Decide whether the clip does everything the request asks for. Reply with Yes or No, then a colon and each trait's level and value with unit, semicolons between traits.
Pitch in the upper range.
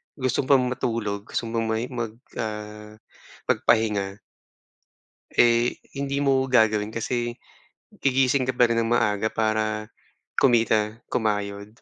No: low, 115 Hz